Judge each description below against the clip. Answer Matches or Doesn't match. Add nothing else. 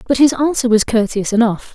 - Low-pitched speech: Doesn't match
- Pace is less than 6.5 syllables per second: Matches